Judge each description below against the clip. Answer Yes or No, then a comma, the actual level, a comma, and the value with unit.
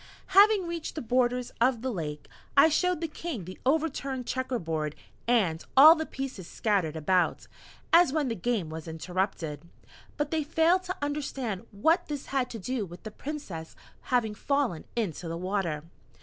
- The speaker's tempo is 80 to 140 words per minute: No, average, 165 wpm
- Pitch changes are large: Yes, wide, 8.4 semitones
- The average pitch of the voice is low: No, high, 245 Hz